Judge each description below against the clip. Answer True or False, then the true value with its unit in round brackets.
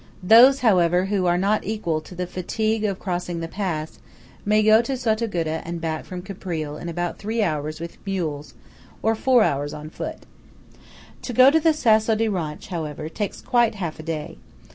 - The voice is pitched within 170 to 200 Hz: True (185 Hz)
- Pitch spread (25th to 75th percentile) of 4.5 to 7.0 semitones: True (4.9 semitones)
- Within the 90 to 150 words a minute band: False (185 wpm)